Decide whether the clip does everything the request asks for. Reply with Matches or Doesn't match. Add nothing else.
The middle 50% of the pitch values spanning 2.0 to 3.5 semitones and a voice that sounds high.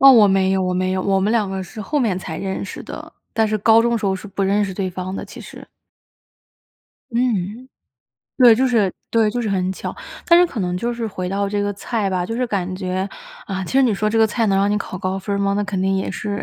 Matches